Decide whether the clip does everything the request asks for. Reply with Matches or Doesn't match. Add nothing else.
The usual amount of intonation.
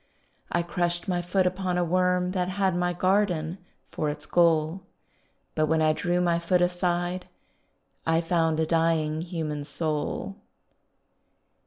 Doesn't match